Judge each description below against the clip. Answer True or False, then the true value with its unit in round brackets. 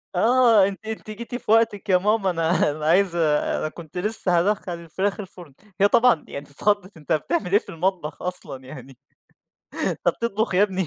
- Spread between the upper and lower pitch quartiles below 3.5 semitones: False (4.2 semitones)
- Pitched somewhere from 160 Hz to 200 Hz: True (190 Hz)